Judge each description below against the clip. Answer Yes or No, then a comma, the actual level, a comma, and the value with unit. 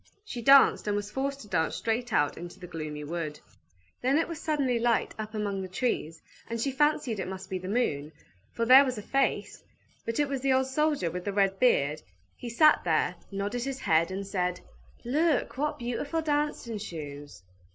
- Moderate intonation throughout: No, wide, 6.9 semitones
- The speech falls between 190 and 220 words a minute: Yes, average, 195 wpm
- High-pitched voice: Yes, high, 225 Hz